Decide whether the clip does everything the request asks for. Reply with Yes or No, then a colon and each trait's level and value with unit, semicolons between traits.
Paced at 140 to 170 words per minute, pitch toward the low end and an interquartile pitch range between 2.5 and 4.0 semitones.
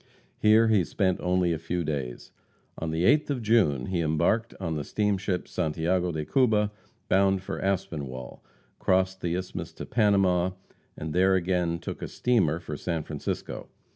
Yes: average, 160 wpm; very low, 90 Hz; average, 3.5 semitones